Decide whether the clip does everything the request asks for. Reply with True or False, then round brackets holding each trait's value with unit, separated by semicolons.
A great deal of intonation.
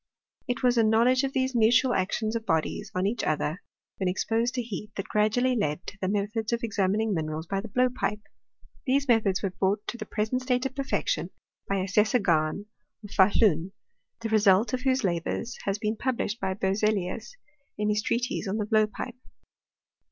False (3.7 semitones)